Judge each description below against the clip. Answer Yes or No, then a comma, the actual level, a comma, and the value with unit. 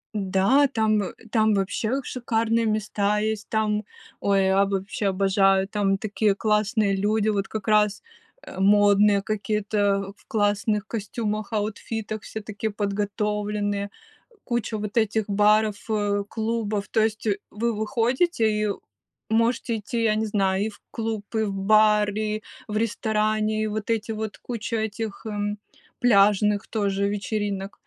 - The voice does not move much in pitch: Yes, narrow, 1.4 semitones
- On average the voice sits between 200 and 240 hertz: Yes, high, 210 Hz